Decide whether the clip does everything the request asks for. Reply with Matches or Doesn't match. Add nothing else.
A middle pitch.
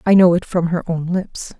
Matches